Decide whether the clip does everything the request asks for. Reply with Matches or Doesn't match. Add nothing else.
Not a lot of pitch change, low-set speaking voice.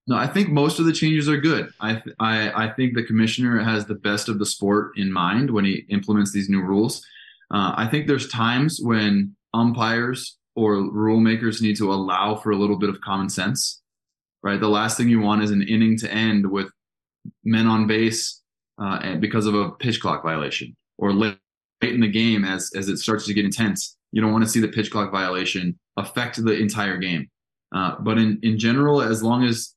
Matches